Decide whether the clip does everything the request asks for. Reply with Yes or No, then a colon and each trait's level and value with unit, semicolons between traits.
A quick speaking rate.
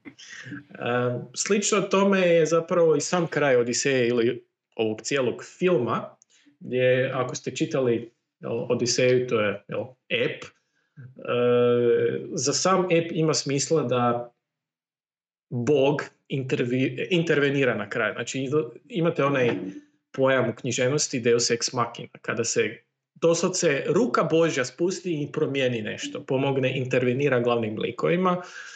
No: average, 120 wpm